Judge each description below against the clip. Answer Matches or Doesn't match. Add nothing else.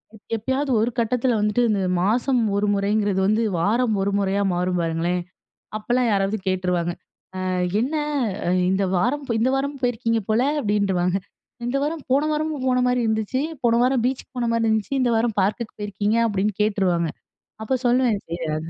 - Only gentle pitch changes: Doesn't match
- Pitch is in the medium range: Doesn't match